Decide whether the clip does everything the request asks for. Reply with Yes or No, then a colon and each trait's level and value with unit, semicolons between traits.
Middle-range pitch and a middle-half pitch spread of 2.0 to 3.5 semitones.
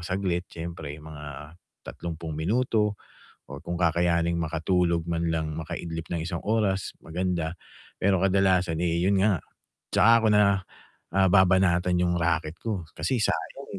No: very low, 85 Hz; narrow, 2.6 semitones